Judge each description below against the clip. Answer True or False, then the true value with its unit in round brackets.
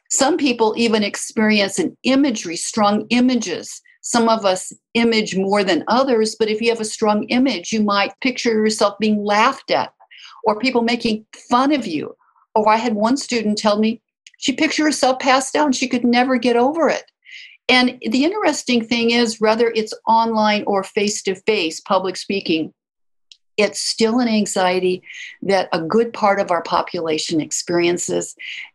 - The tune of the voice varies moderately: True (3.5 semitones)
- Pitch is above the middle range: True (225 Hz)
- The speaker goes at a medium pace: True (165 wpm)